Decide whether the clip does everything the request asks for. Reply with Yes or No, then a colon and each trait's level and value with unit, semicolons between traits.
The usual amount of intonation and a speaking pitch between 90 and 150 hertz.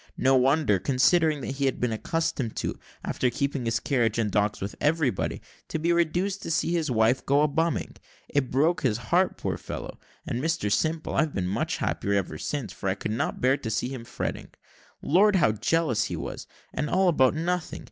No: wide, 6.2 semitones; low, 135 Hz